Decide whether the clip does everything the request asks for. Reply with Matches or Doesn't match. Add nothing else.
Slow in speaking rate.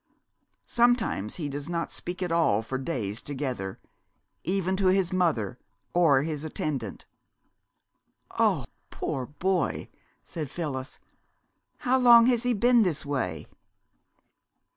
Matches